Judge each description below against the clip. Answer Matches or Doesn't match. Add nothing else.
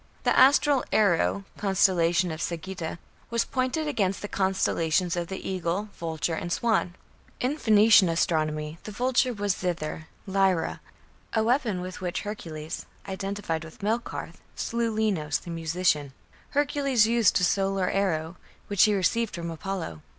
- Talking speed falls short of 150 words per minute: Matches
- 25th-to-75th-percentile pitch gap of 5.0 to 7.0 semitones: Doesn't match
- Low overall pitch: Doesn't match